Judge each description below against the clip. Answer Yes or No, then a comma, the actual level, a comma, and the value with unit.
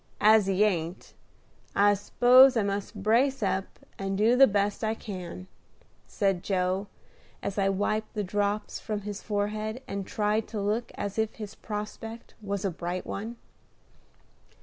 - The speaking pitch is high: Yes, high, 205 Hz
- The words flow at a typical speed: Yes, average, 150 wpm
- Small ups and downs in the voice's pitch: Yes, narrow, 1.8 semitones